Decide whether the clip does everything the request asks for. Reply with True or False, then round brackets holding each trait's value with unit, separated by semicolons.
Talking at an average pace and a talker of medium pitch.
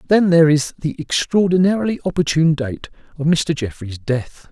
True (145 wpm; 160 Hz)